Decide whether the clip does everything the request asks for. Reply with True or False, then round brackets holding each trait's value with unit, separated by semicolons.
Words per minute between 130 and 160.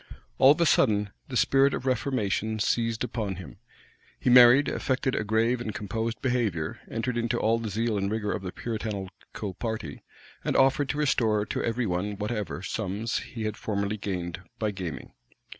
False (170 wpm)